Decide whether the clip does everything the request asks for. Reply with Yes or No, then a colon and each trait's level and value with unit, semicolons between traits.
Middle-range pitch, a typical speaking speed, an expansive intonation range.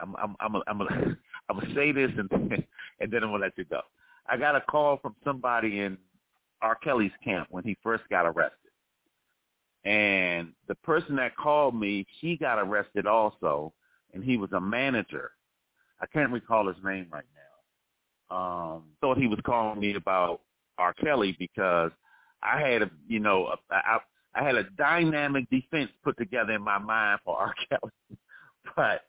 No: low, 110 Hz; average, 175 wpm; wide, 6.6 semitones